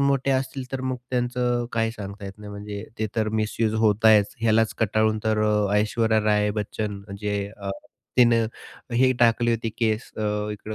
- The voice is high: No, low, 110 Hz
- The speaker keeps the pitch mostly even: Yes, narrow, 2.2 semitones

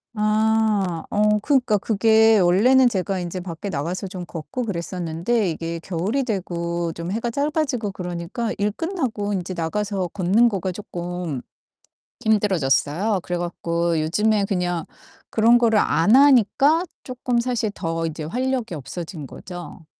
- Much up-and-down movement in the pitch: No, average, 4.5 semitones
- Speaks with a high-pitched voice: Yes, high, 195 Hz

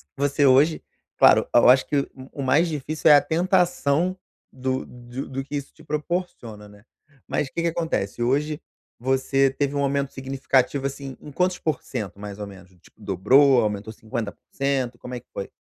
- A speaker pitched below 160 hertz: Yes, low, 135 Hz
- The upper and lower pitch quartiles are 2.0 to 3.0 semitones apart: No, average, 3.5 semitones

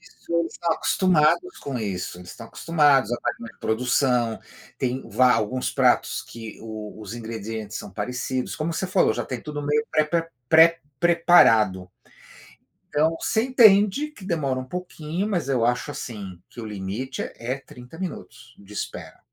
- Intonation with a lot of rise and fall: Yes, wide, 6.7 semitones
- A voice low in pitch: Yes, low, 130 Hz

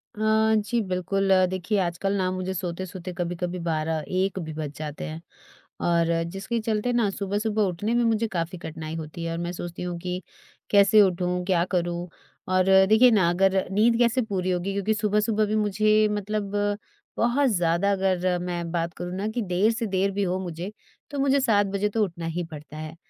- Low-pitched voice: No, medium, 185 Hz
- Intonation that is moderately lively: Yes, average, 3.5 semitones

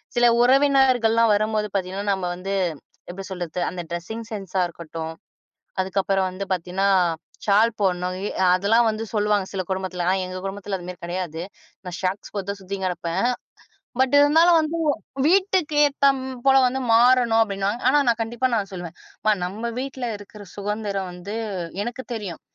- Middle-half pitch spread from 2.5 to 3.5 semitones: No, average, 4.1 semitones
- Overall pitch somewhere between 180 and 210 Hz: Yes, high, 200 Hz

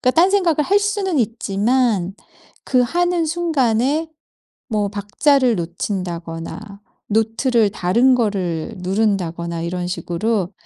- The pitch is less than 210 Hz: No, high, 220 Hz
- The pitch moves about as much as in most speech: No, wide, 7.2 semitones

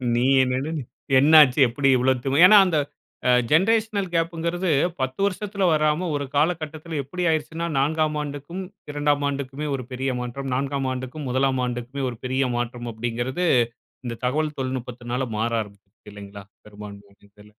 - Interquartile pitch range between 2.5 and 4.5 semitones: Yes, average, 4.2 semitones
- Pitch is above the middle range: No, low, 135 Hz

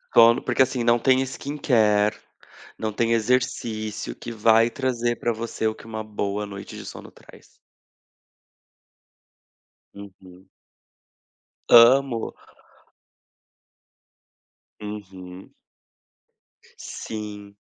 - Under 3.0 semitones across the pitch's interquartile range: Yes, narrow, 2.5 semitones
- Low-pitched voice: Yes, low, 110 Hz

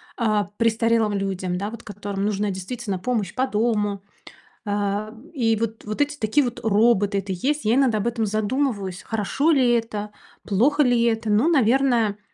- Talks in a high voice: Yes, high, 220 Hz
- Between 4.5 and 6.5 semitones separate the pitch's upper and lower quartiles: No, average, 2.8 semitones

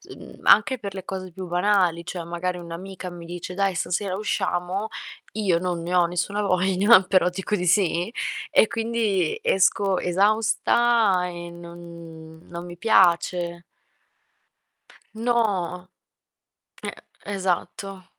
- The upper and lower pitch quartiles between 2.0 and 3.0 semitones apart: Yes, narrow, 2.5 semitones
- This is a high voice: No, medium, 180 Hz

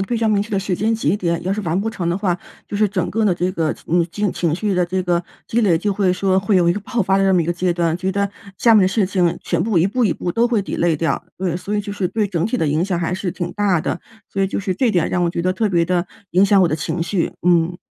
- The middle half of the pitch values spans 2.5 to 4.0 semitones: Yes, average, 2.8 semitones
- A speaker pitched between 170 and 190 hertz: Yes, medium, 185 Hz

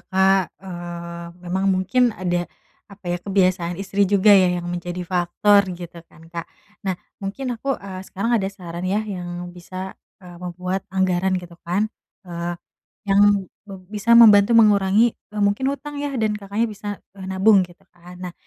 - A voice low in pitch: No, high, 190 Hz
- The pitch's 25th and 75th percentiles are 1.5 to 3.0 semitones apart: Yes, average, 2.7 semitones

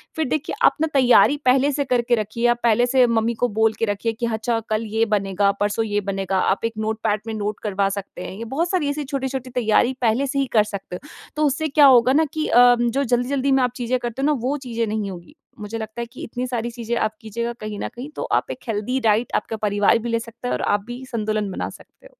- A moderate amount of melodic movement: Yes, average, 3.2 semitones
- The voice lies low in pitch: No, high, 235 Hz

